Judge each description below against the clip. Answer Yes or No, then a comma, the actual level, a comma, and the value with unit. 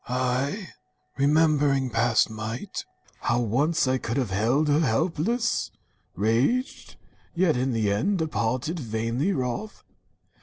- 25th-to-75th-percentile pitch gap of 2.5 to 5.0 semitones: No, wide, 5.5 semitones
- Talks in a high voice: No, low, 130 Hz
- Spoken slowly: Yes, slow, 125 wpm